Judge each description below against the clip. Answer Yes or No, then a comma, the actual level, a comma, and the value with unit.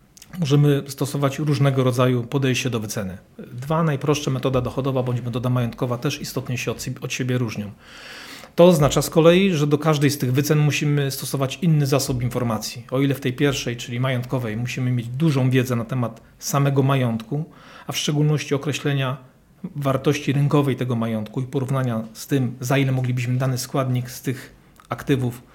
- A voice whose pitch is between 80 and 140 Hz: Yes, low, 135 Hz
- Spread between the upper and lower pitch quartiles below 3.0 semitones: Yes, narrow, 2.5 semitones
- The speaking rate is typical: No, fast, 170 wpm